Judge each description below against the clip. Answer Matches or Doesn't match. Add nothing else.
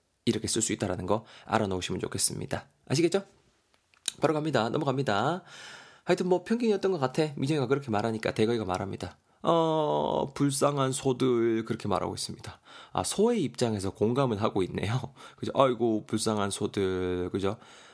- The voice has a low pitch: Matches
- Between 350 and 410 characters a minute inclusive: Matches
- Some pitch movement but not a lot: Doesn't match